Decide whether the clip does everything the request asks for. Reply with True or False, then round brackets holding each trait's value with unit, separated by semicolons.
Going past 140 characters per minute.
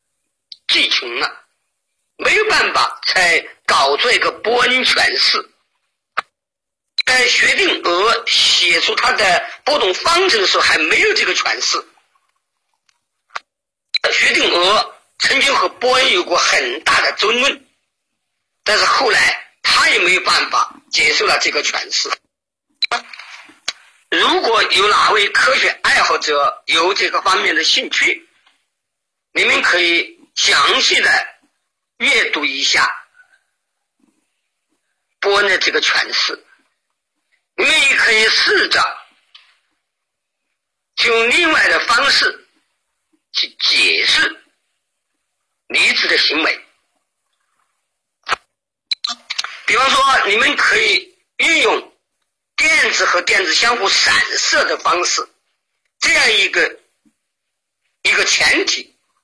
True (160 characters per minute)